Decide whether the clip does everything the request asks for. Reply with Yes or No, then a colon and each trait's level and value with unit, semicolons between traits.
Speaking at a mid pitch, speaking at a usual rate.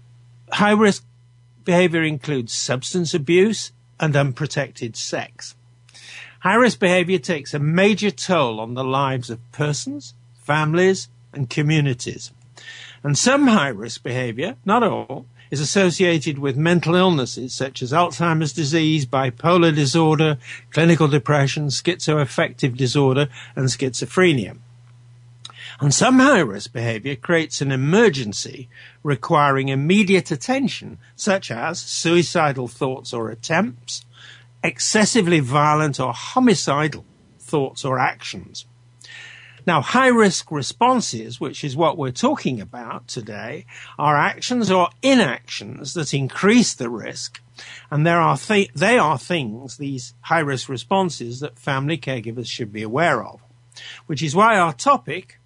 No: medium, 145 Hz; slow, 125 wpm